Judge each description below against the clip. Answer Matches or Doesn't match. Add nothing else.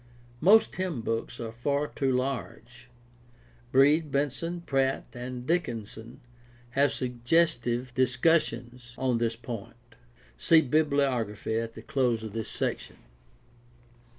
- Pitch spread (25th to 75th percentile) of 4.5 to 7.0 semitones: Doesn't match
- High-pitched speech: Doesn't match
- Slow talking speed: Matches